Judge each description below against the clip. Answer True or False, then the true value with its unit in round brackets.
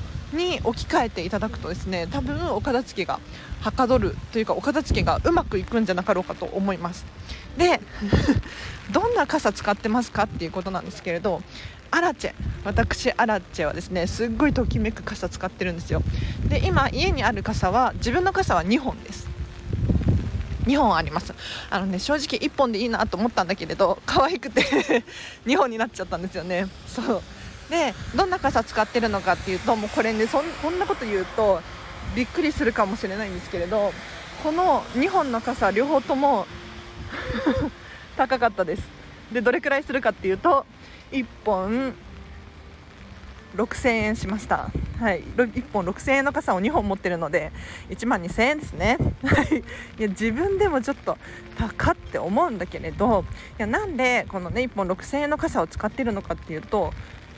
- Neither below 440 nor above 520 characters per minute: False (325 characters per minute)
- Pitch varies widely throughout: True (6.3 semitones)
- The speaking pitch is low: False (220 Hz)